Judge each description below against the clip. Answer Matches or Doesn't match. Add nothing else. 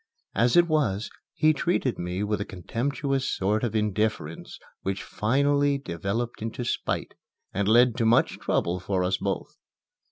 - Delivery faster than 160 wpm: Doesn't match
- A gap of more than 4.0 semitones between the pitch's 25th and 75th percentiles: Matches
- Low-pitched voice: Matches